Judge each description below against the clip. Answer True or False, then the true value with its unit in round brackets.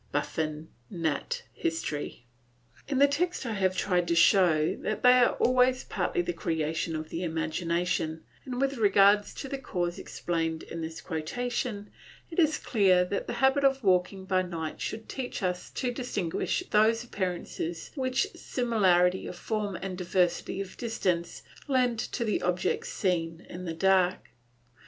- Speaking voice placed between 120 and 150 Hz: False (190 Hz)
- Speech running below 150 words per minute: False (155 wpm)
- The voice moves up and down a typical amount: False (6.4 semitones)